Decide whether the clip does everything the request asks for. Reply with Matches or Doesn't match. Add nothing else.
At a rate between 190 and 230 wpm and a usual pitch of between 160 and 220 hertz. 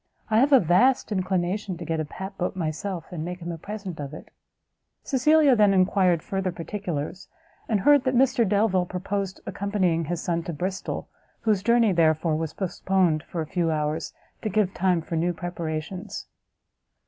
Doesn't match